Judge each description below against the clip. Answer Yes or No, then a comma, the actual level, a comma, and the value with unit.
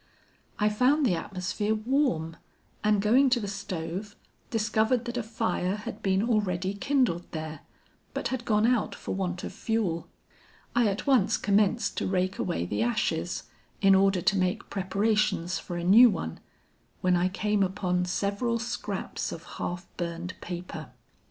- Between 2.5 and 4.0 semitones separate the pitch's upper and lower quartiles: Yes, average, 3.6 semitones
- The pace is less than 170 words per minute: Yes, average, 155 wpm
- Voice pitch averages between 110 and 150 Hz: No, high, 200 Hz